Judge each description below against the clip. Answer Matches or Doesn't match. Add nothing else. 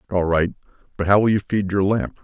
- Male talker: Matches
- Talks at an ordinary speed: Doesn't match